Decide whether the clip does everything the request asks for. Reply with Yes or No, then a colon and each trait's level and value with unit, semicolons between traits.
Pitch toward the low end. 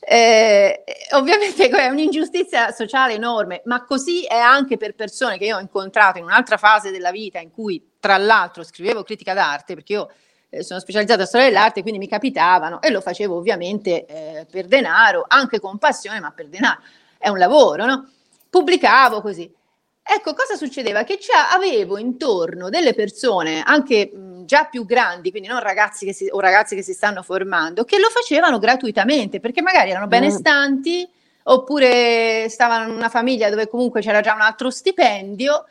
No: high, 225 Hz